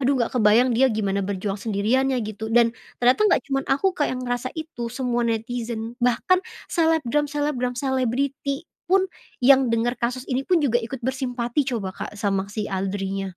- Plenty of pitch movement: No, average, 3.4 semitones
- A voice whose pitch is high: Yes, high, 245 Hz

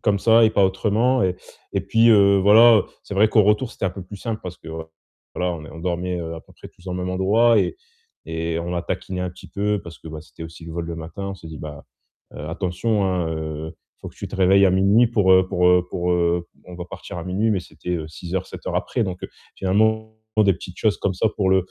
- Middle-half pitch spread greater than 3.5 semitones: No, average, 3.2 semitones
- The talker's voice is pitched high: No, very low, 95 Hz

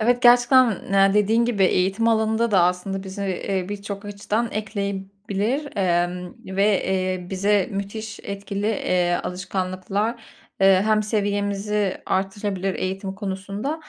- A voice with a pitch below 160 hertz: No, high, 200 Hz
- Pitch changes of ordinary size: No, narrow, 2.1 semitones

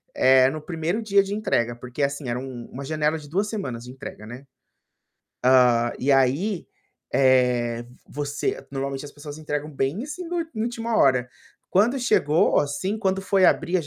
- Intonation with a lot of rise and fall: Yes, wide, 6.7 semitones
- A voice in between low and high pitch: Yes, medium, 145 Hz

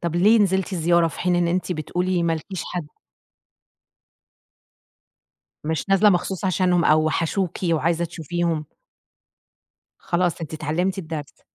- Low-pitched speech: No, medium, 175 Hz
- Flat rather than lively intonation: Yes, narrow, 2.3 semitones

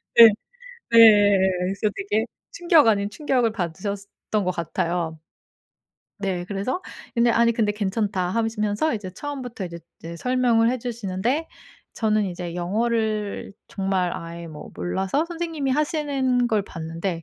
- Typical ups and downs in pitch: Yes, average, 4.8 semitones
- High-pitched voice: Yes, high, 210 Hz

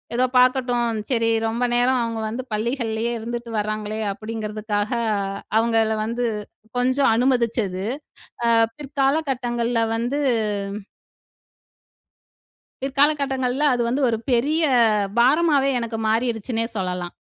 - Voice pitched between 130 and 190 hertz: No, high, 235 Hz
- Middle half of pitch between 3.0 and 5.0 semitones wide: No, narrow, 2.6 semitones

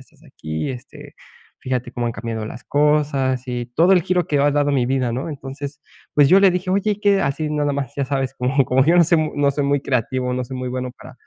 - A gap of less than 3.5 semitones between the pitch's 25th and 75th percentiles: Yes, average, 2.9 semitones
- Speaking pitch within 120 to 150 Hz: Yes, medium, 140 Hz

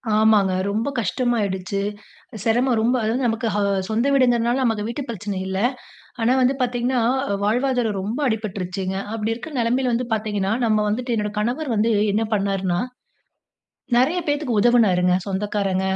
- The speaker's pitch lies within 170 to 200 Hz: No, high, 225 Hz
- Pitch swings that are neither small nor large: Yes, average, 3.2 semitones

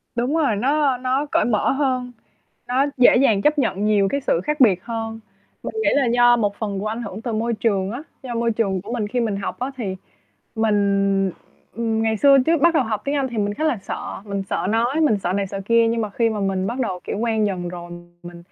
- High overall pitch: Yes, high, 225 Hz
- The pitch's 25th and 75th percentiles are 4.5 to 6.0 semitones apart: No, average, 3.9 semitones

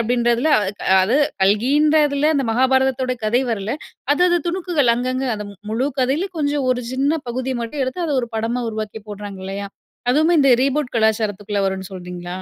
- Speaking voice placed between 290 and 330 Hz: No, very high, 250 Hz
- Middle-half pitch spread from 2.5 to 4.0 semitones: No, average, 4.8 semitones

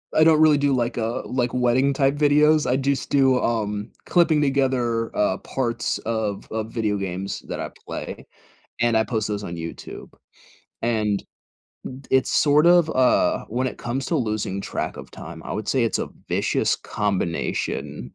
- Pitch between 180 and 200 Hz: No, low, 120 Hz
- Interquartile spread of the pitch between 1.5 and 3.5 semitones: No, average, 4.5 semitones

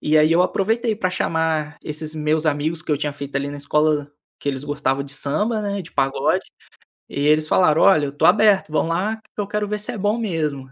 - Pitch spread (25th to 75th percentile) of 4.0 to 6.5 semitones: Yes, average, 5.1 semitones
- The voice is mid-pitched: Yes, medium, 155 Hz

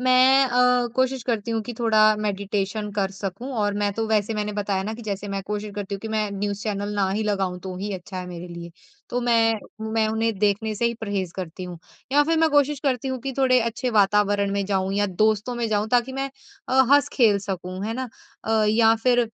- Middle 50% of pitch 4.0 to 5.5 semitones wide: No, average, 3.2 semitones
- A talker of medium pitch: No, high, 215 Hz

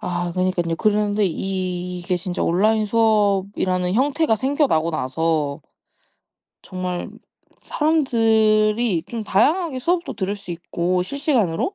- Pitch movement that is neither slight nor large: Yes, average, 4.3 semitones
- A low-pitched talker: No, high, 200 Hz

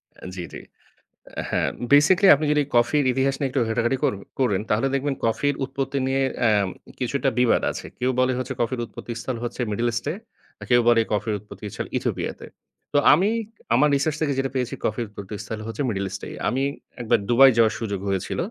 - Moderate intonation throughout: Yes, average, 3.4 semitones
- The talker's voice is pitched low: Yes, low, 125 Hz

